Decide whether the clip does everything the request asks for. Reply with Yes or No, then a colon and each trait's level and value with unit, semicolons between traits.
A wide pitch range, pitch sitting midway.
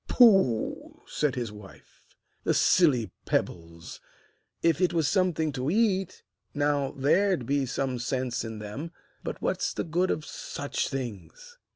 Yes: wide, 6.4 semitones; medium, 145 Hz